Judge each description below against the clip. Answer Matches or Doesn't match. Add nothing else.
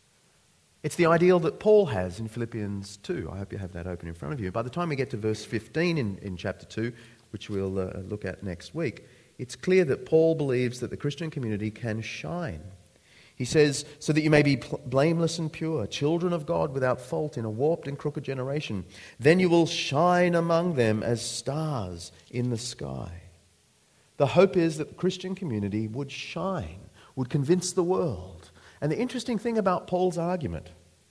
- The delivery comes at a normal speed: Matches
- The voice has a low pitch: Matches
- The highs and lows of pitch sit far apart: Matches